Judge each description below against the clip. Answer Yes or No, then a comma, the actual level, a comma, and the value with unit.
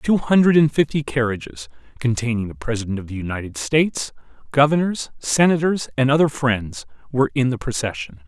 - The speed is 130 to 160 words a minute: Yes, average, 150 wpm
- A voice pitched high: No, low, 125 Hz